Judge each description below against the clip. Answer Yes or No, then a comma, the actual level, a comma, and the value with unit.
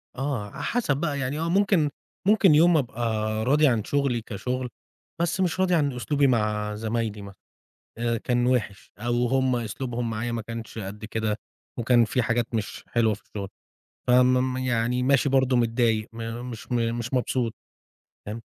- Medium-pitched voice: No, low, 120 Hz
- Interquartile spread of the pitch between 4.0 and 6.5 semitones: No, average, 2.9 semitones